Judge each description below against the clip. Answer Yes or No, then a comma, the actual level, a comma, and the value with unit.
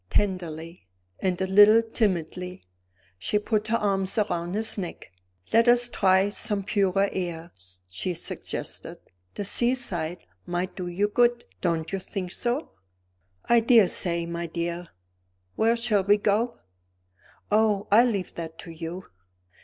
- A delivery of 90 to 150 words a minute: Yes, slow, 135 wpm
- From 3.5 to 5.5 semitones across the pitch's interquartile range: Yes, average, 3.8 semitones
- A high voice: Yes, high, 195 Hz